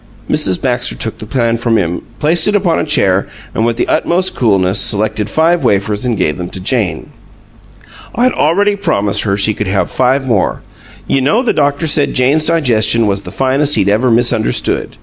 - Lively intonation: Yes, wide, 6.4 semitones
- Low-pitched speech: Yes, low, 120 Hz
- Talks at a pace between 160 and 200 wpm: Yes, average, 190 wpm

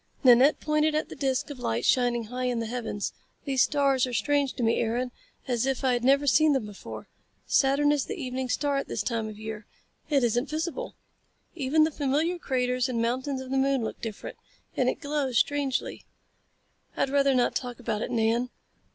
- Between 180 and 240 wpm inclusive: Yes, average, 200 wpm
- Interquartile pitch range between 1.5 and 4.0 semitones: Yes, average, 2.9 semitones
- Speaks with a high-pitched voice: Yes, very high, 260 Hz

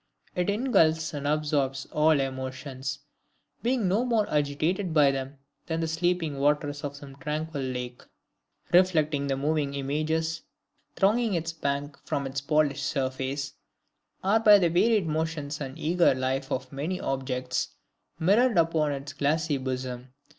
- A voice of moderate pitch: Yes, medium, 150 Hz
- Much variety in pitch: No, average, 3.2 semitones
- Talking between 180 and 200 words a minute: No, average, 140 wpm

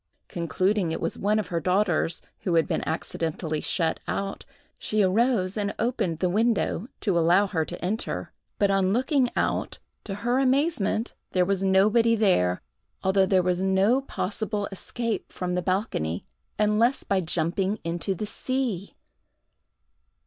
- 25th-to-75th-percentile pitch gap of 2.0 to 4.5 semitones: Yes, average, 3.4 semitones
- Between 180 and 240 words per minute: No, average, 150 wpm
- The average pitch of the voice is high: Yes, high, 195 Hz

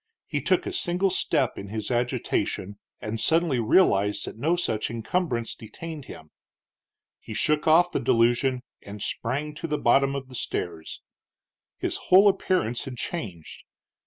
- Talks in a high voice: No, low, 130 Hz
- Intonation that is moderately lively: No, wide, 6.9 semitones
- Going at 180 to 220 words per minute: No, average, 150 wpm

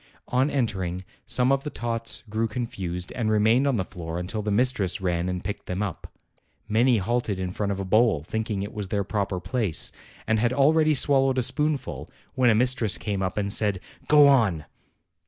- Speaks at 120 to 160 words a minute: No, average, 195 wpm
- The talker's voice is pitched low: Yes, low, 110 Hz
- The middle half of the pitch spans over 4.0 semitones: Yes, average, 4.9 semitones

